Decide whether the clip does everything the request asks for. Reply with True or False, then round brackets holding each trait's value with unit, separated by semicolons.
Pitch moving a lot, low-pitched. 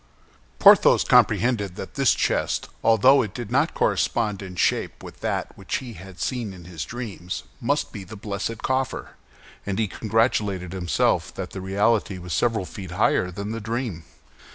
False (3.7 semitones; 105 Hz)